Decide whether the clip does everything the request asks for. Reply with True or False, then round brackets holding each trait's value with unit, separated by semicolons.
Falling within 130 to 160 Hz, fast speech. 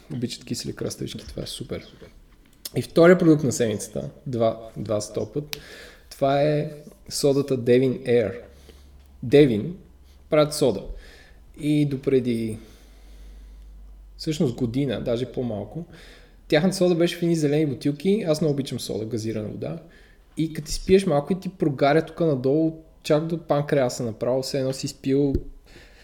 False (140 Hz; 135 wpm)